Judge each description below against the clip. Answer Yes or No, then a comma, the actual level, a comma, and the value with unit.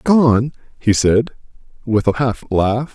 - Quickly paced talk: No, average, 145 wpm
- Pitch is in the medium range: No, low, 120 Hz